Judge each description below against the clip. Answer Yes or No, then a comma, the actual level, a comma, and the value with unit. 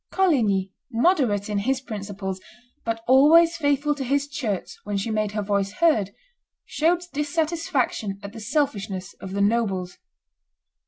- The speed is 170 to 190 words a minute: No, average, 140 wpm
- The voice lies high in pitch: Yes, high, 225 Hz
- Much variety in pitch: Yes, wide, 6.3 semitones